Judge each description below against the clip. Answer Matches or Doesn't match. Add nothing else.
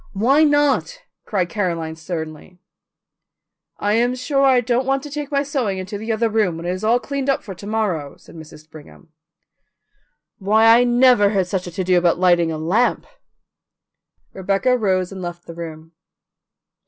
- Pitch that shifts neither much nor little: Doesn't match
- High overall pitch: Matches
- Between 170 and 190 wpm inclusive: Matches